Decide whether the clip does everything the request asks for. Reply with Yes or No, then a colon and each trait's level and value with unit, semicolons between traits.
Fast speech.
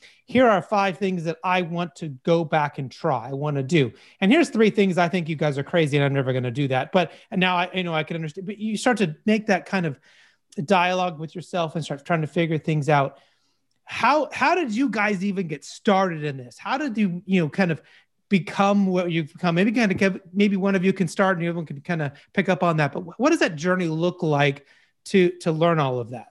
Yes: fast, 260 wpm